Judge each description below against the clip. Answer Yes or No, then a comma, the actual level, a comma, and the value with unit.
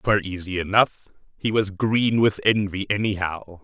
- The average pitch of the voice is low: Yes, low, 100 Hz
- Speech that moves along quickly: No, average, 150 wpm